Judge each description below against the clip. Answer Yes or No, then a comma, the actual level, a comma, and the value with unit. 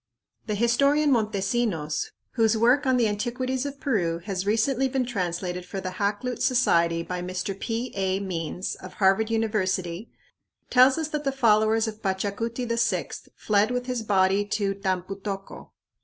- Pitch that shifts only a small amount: No, average, 4.3 semitones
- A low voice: No, high, 215 Hz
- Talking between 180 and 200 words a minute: No, average, 155 wpm